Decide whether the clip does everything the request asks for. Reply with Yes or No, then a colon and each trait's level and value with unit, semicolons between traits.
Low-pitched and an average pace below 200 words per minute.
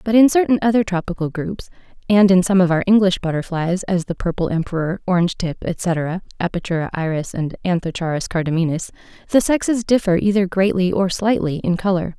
No: medium, 185 Hz; average, 165 wpm